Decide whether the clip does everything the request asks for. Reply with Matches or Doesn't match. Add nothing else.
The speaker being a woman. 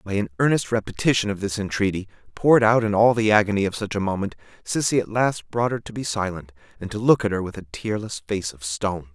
Doesn't match